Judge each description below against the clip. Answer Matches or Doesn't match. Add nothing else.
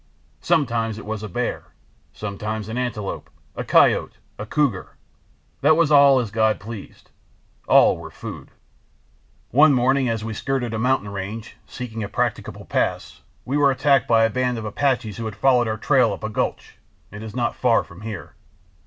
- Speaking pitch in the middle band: Doesn't match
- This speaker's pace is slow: Doesn't match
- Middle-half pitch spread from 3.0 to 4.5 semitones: Matches